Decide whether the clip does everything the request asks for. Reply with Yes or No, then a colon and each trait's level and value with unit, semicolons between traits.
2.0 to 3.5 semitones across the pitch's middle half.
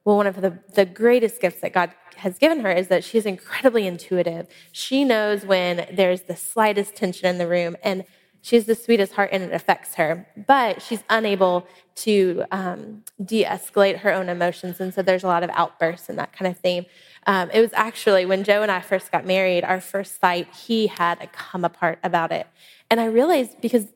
Yes: average, 2.9 semitones